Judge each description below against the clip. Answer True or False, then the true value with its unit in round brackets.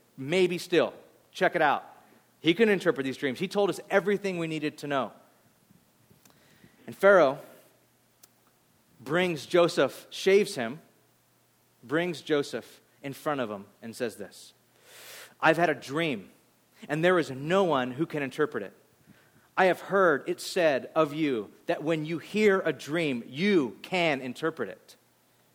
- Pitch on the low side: False (160 Hz)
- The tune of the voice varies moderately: True (4.2 semitones)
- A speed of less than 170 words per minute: True (150 wpm)